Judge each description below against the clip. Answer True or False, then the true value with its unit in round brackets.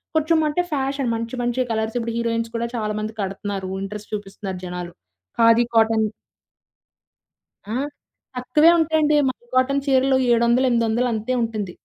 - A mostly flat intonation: False (3.2 semitones)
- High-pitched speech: True (230 Hz)